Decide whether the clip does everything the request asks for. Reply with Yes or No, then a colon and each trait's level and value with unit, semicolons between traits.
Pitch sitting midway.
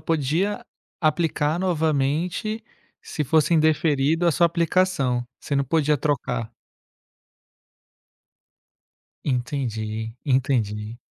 Yes: medium, 150 Hz